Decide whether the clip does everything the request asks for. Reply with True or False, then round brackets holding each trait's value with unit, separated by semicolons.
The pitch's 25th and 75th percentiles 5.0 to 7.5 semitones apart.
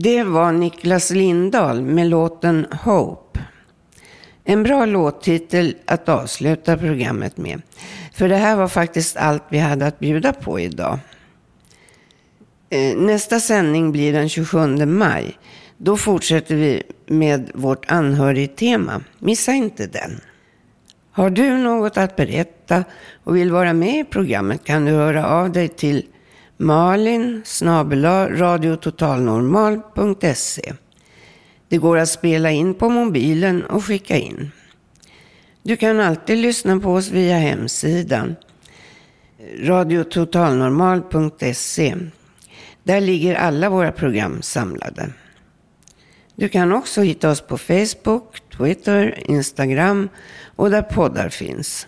False (4.4 semitones)